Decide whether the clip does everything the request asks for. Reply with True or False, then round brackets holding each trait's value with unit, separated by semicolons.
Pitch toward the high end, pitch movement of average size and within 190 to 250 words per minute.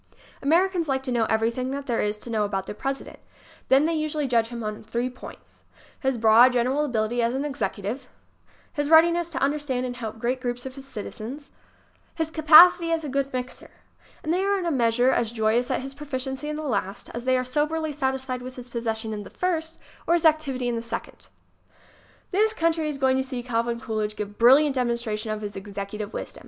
True (255 Hz; 4.5 semitones; 205 wpm)